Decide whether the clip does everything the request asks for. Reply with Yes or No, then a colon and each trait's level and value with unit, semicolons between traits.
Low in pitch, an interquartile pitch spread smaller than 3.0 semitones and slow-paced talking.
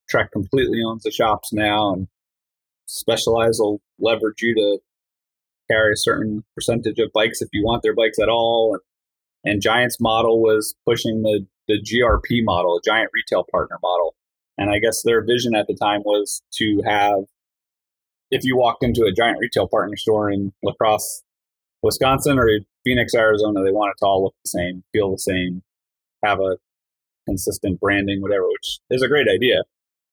No: low, 105 Hz; narrow, 2.4 semitones; average, 175 wpm